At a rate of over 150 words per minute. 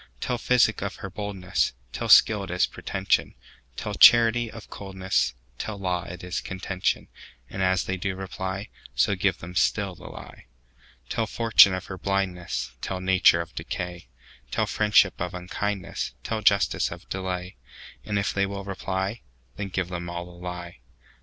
No: slow, 135 wpm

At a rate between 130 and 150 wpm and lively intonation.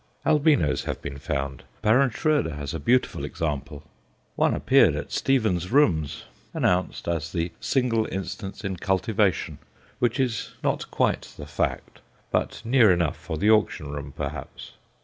Yes: average, 145 wpm; wide, 7.4 semitones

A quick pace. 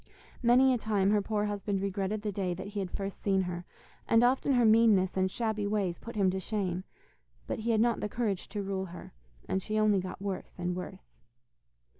Yes: fast, 210 wpm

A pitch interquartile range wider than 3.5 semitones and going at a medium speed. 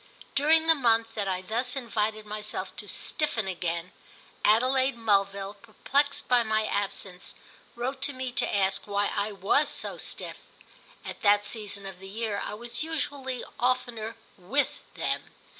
Yes: average, 4.1 semitones; average, 150 wpm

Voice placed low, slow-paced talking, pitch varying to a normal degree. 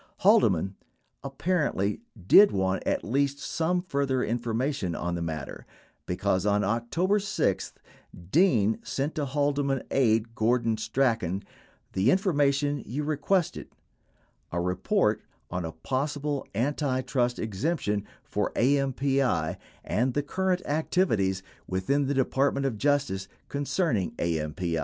No: low, 130 Hz; slow, 115 wpm; wide, 6.2 semitones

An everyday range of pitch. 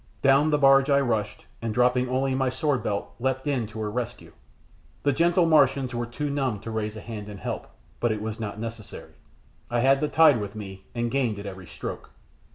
Yes: average, 4.0 semitones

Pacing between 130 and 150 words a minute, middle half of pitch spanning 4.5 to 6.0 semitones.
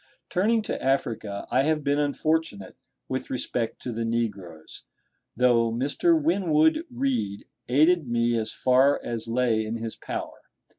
Yes: average, 140 wpm; wide, 5.5 semitones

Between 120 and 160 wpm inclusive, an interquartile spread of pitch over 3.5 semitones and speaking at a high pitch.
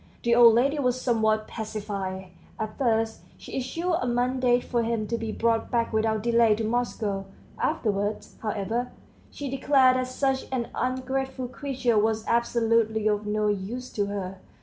No: average, 155 wpm; average, 2.9 semitones; high, 230 Hz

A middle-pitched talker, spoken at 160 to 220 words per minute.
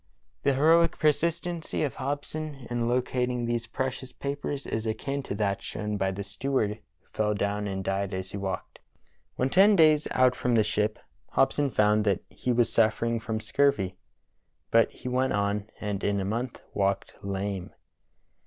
No: low, 115 Hz; average, 165 wpm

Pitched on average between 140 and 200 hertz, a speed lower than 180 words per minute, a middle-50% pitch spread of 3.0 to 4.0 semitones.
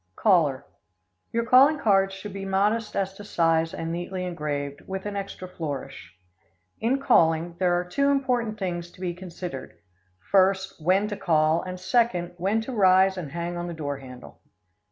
Yes: medium, 185 Hz; average, 170 wpm; average, 3.4 semitones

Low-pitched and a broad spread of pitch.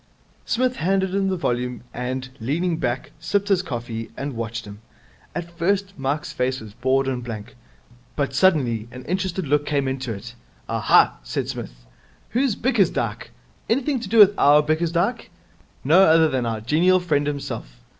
No: medium, 145 Hz; wide, 7.2 semitones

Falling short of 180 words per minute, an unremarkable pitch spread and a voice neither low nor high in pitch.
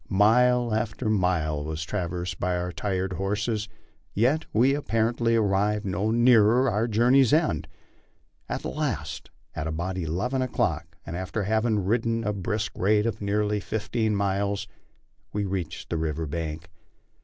No: average, 145 wpm; average, 4.1 semitones; low, 105 Hz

